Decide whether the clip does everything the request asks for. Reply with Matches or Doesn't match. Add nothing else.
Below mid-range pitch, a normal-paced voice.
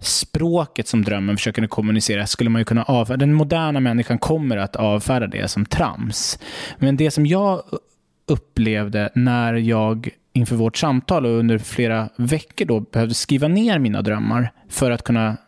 Matches